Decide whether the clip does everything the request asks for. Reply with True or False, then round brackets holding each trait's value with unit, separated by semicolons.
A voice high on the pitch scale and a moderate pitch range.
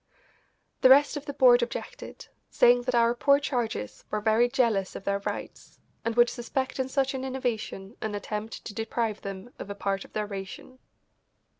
True (235 Hz; 3.8 semitones)